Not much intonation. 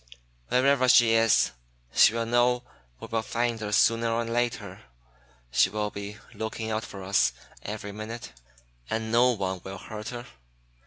Yes: narrow, 2.2 semitones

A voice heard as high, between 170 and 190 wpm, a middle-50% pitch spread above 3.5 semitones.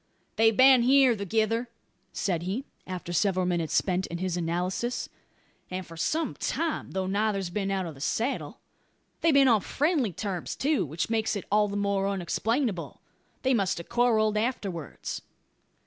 No: high, 200 Hz; average, 160 wpm; average, 4.7 semitones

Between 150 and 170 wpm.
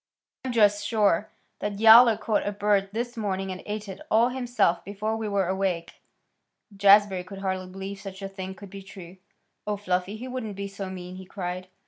No: average, 185 wpm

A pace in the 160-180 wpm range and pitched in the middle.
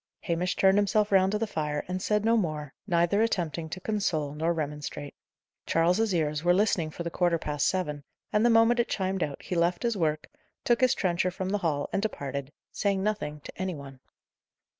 No: average, 200 wpm; medium, 175 Hz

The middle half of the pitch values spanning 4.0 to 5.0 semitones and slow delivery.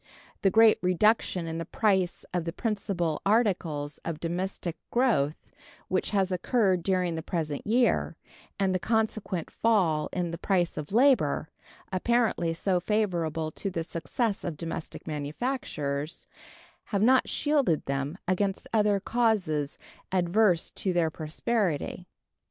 Yes: average, 4.6 semitones; slow, 130 wpm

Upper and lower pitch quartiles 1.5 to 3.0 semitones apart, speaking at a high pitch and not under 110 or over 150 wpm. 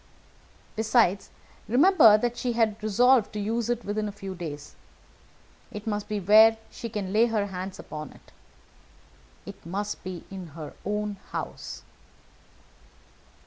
Yes: average, 2.7 semitones; high, 210 Hz; average, 140 wpm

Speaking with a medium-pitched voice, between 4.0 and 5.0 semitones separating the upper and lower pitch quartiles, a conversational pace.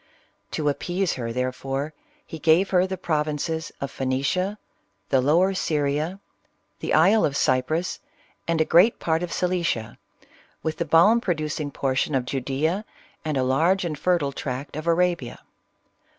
Yes: medium, 155 Hz; average, 4.3 semitones; average, 160 wpm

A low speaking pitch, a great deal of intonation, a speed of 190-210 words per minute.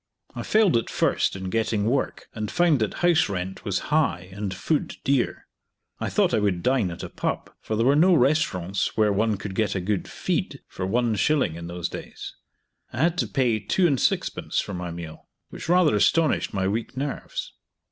Yes: low, 110 Hz; wide, 7.2 semitones; average, 195 wpm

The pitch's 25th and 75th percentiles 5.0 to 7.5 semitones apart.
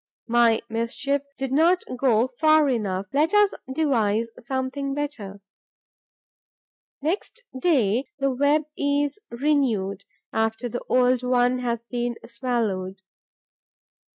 No: average, 3.9 semitones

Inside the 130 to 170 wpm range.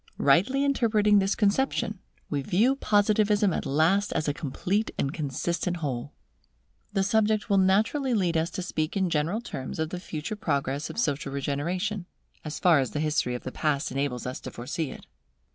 No: average, 180 wpm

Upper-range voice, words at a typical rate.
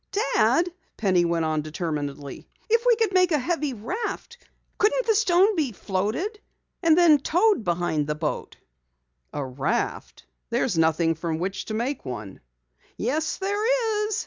Yes: high, 245 Hz; average, 150 wpm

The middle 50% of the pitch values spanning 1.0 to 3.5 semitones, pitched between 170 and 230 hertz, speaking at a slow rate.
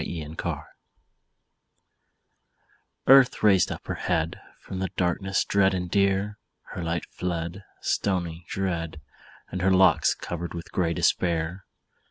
No: narrow, 2.4 semitones; very low, 90 Hz; slow, 125 wpm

